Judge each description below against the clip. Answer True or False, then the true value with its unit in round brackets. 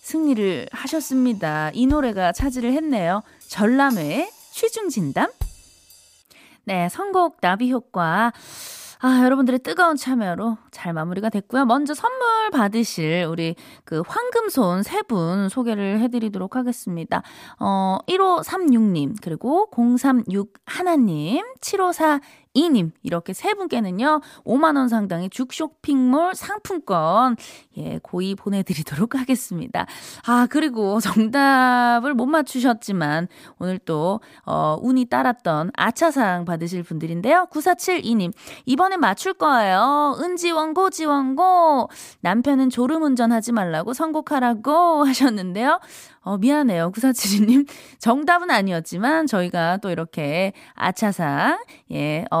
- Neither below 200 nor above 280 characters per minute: True (250 characters per minute)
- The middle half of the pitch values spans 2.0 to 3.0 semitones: False (8.0 semitones)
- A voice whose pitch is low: False (250 Hz)